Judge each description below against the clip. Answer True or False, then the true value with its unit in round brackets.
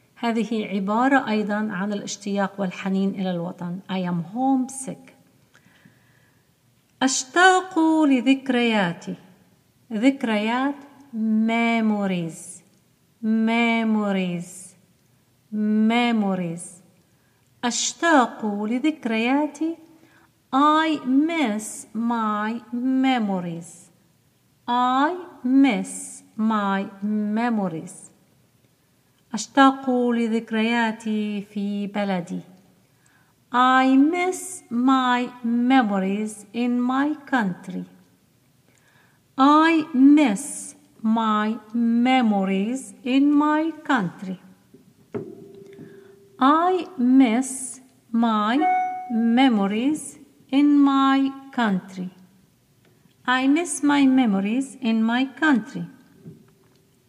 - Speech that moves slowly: True (60 wpm)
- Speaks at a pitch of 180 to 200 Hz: False (230 Hz)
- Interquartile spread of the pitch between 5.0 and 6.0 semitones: True (5.3 semitones)